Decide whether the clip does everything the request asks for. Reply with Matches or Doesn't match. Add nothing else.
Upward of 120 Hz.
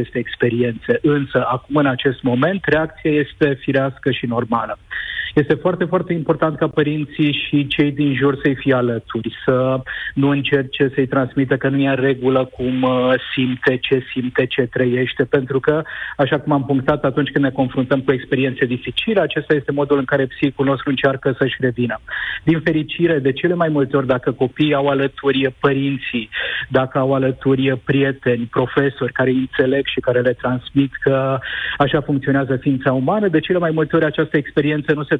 Matches